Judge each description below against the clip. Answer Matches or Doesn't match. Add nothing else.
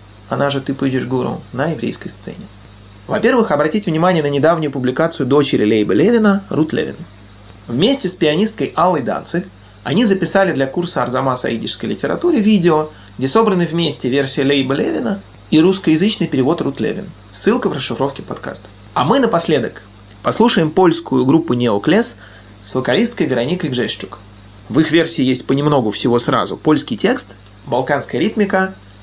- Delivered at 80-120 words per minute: Doesn't match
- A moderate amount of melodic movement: Doesn't match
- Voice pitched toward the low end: Doesn't match